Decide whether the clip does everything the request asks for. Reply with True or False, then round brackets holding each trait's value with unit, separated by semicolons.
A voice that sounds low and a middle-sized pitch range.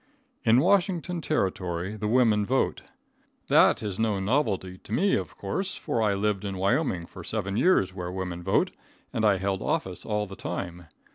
True (105 Hz; 4.1 semitones)